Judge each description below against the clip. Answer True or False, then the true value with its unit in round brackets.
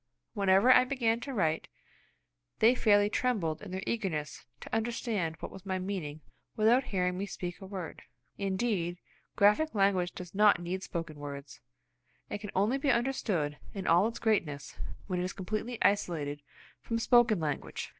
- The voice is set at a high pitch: True (195 Hz)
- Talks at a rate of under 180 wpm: True (160 wpm)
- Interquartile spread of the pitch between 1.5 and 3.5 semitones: False (4.4 semitones)